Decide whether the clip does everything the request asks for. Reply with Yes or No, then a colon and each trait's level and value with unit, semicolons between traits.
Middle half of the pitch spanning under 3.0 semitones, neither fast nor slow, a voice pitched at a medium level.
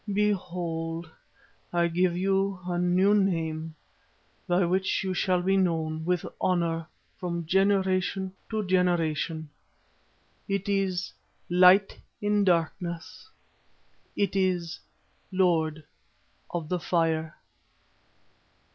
No: narrow, 2.4 semitones; slow, 95 wpm; medium, 180 Hz